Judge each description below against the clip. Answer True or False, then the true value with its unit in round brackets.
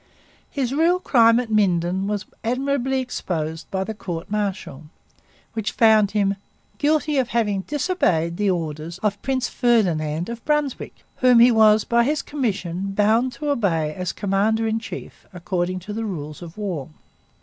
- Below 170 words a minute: True (155 wpm)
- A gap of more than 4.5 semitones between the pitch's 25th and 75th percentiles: True (5.2 semitones)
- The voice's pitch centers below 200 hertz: False (210 Hz)